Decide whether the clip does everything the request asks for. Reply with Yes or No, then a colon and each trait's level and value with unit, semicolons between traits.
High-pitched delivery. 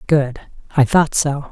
No: medium, 145 Hz